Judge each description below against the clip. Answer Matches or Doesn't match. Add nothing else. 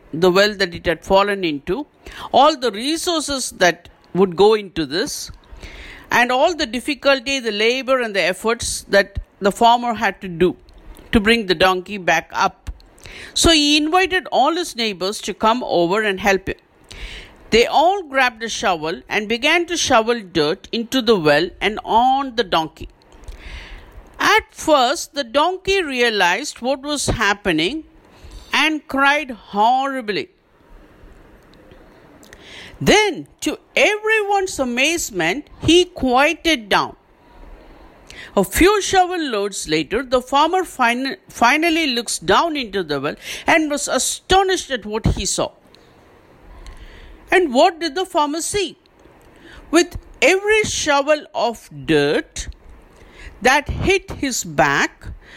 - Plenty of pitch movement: Matches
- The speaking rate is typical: Doesn't match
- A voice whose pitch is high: Matches